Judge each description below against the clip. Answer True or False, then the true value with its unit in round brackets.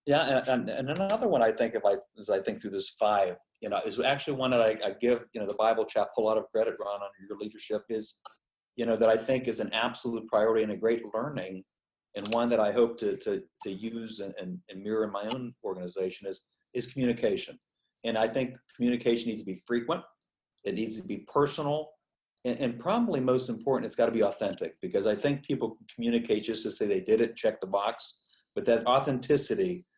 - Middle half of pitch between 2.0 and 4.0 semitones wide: False (5.1 semitones)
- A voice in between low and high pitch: False (120 Hz)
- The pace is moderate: False (225 wpm)